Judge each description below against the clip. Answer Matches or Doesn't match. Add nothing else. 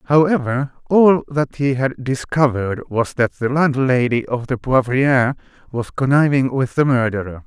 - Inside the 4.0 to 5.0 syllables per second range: Matches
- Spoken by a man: Matches